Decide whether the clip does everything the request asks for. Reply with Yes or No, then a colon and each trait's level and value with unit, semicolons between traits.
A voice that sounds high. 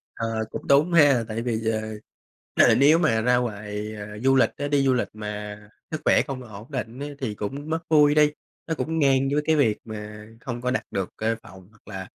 No: low, 120 Hz